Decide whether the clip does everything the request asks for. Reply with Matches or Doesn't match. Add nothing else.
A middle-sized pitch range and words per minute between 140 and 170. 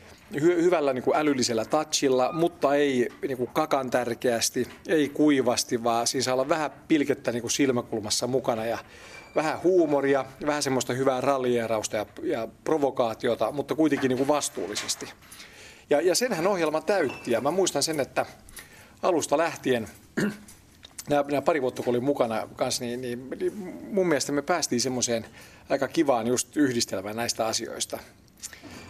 Matches